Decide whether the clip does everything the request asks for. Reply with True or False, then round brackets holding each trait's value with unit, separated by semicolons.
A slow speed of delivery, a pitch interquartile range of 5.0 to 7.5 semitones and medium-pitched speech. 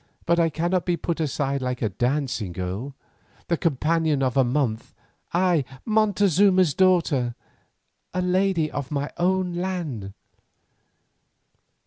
True (120 wpm; 5.6 semitones; 160 Hz)